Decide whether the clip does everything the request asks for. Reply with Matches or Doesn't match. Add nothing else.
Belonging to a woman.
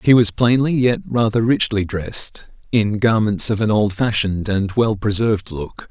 Doesn't match